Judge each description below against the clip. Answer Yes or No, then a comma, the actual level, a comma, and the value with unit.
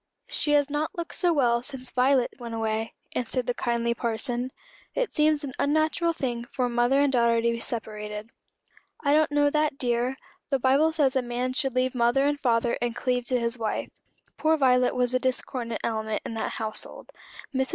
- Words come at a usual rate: Yes, average, 190 wpm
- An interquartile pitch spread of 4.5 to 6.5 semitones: No, average, 3.2 semitones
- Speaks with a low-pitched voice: No, very high, 250 Hz